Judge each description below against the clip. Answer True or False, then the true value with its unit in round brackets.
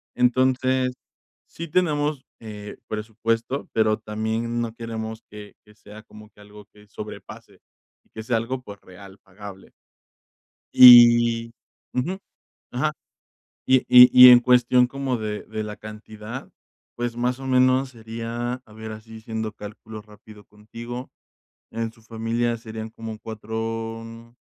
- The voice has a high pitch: False (115 Hz)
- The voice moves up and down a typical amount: False (2.2 semitones)